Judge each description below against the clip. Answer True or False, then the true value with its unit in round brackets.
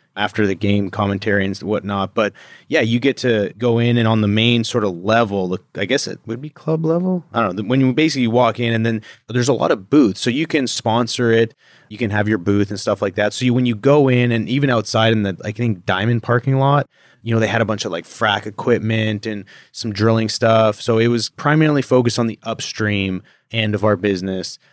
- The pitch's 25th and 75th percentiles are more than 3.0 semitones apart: False (2.7 semitones)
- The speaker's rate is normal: False (240 wpm)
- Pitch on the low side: True (115 Hz)